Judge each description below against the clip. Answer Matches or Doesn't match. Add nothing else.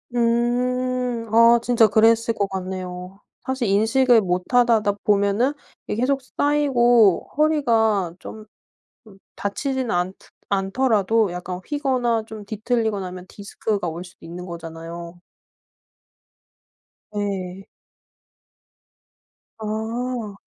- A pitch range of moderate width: Matches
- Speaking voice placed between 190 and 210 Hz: Doesn't match